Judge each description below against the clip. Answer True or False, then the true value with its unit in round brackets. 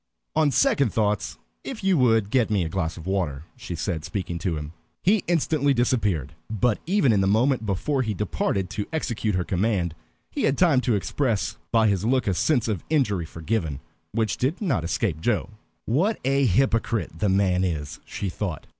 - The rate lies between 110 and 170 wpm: False (185 wpm)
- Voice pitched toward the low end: True (105 Hz)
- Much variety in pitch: True (6.4 semitones)